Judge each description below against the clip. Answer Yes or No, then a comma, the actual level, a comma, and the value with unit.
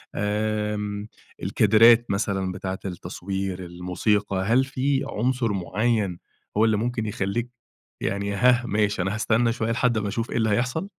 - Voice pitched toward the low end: Yes, low, 105 Hz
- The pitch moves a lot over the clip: No, average, 3.1 semitones